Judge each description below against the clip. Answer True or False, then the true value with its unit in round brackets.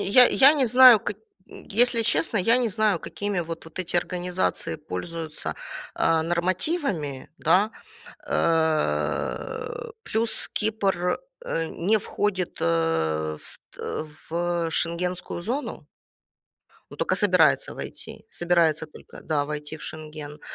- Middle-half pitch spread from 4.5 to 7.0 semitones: True (5.5 semitones)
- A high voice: False (175 Hz)